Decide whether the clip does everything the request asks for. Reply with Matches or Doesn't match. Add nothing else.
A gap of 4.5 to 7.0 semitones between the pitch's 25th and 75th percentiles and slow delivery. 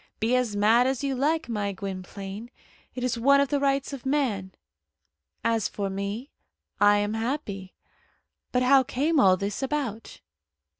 Doesn't match